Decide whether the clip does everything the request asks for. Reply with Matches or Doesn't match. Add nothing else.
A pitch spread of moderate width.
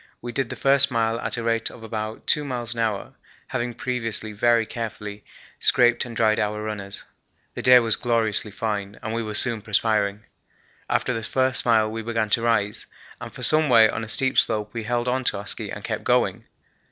Doesn't match